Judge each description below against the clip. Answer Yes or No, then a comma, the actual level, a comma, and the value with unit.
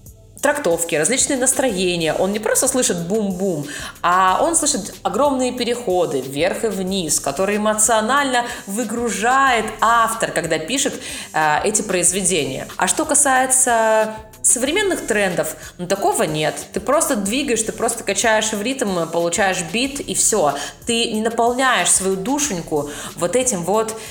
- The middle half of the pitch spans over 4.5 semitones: Yes, wide, 5.4 semitones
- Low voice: No, high, 220 Hz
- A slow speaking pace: No, average, 130 wpm